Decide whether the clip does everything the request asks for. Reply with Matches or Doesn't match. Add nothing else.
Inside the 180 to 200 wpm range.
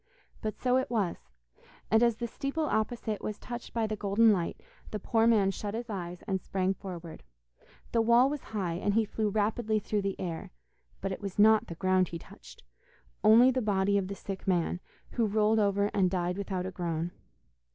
Matches